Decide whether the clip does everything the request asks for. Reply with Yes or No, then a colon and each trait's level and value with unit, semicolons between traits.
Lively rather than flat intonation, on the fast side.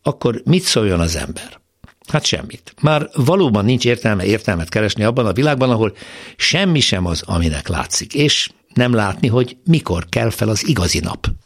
Yes: wide, 6.1 semitones; fast, 170 wpm